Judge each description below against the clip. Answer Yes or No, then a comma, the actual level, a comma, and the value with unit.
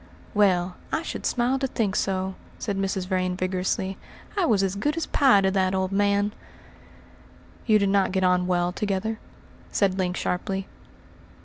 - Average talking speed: Yes, average, 165 wpm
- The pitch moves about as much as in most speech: No, narrow, 1.8 semitones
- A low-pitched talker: No, high, 195 Hz